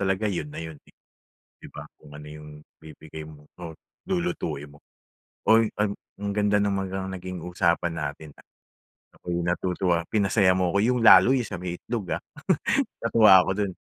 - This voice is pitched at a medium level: No, very low, 90 Hz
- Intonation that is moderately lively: Yes, average, 4.0 semitones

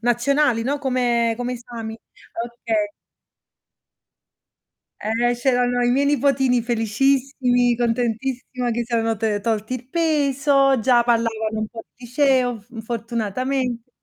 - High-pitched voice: Yes, high, 245 Hz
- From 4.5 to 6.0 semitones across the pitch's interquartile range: No, narrow, 2.5 semitones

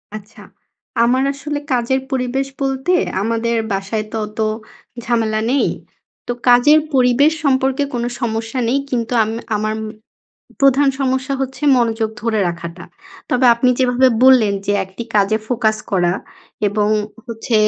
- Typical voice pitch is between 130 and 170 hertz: No, high, 240 Hz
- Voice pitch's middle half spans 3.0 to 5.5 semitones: Yes, average, 3.3 semitones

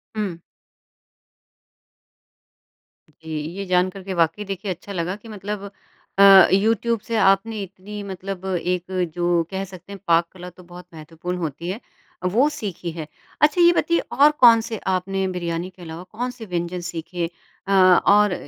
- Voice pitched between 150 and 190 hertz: Yes, medium, 185 Hz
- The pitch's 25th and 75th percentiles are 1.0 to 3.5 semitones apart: Yes, average, 2.8 semitones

